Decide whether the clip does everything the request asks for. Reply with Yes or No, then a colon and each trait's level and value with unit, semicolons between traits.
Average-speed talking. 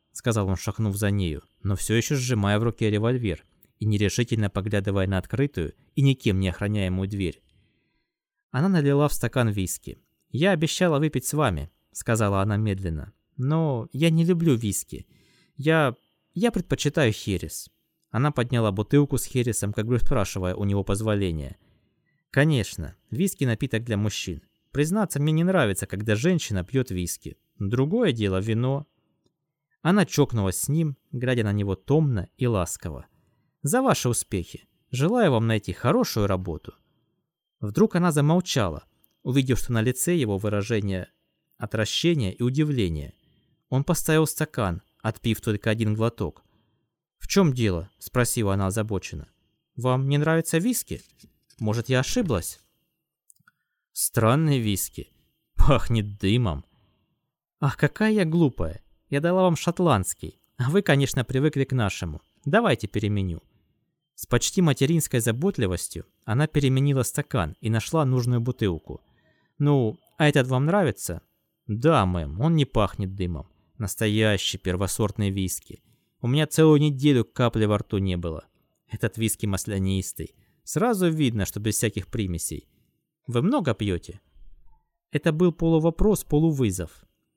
Yes: average, 130 wpm